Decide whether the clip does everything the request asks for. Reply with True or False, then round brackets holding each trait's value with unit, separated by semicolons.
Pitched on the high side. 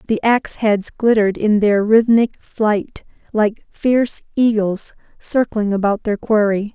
True (215 Hz)